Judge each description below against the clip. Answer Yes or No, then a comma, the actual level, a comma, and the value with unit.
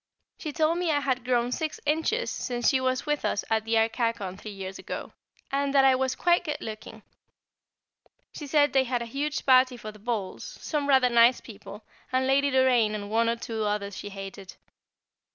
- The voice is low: No, very high, 250 Hz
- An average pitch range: Yes, average, 4.2 semitones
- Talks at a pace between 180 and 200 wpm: Yes, average, 190 wpm